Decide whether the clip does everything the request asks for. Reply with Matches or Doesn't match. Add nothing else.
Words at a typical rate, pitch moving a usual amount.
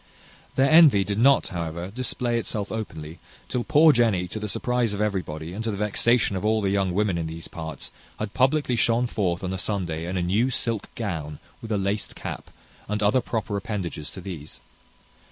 Matches